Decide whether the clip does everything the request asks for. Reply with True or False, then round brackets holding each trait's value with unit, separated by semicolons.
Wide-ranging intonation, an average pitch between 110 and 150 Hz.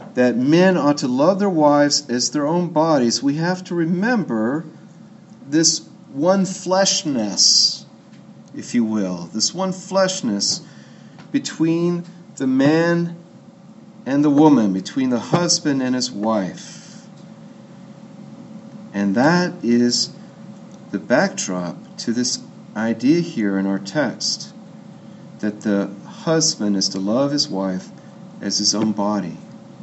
False (8.6 semitones; 165 Hz)